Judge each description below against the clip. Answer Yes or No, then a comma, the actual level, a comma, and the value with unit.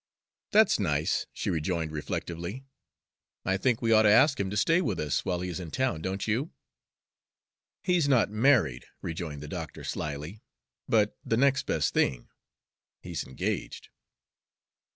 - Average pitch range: No, wide, 7.4 semitones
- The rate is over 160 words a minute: No, average, 150 wpm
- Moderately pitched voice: No, very low, 95 Hz